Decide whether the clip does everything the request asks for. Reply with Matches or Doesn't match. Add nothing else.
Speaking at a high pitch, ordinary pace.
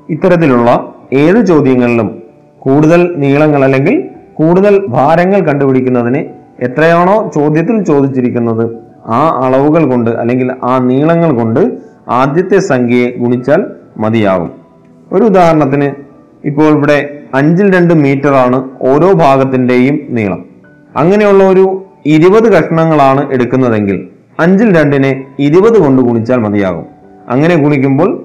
Doesn't match